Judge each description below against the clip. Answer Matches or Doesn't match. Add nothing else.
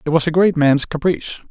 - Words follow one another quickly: Matches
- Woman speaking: Doesn't match